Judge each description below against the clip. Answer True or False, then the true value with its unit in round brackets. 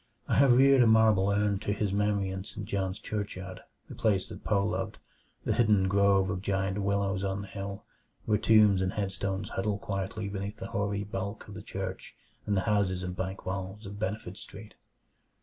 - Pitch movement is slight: True (1.5 semitones)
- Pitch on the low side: True (100 Hz)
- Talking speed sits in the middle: True (190 wpm)